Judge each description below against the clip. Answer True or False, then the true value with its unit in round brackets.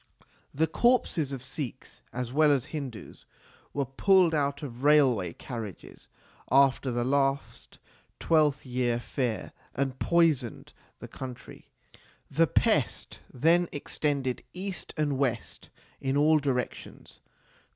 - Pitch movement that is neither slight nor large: True (3.3 semitones)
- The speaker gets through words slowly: True (115 wpm)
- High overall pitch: False (140 Hz)